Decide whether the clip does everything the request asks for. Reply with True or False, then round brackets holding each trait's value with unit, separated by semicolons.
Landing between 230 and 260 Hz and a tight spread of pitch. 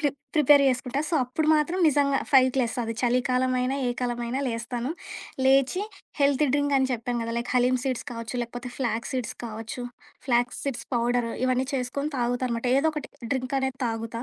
True (255 Hz; 2.2 semitones)